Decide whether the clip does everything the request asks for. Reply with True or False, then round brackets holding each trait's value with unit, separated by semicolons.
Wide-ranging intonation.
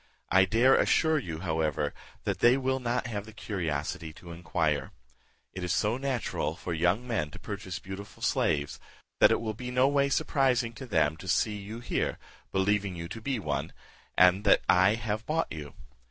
True (6.1 semitones)